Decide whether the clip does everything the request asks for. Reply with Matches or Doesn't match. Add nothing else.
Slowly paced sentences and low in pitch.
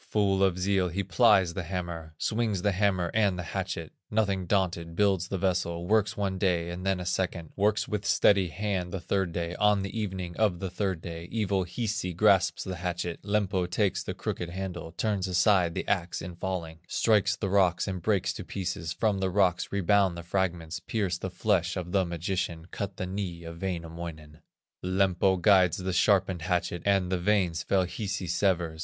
Doesn't match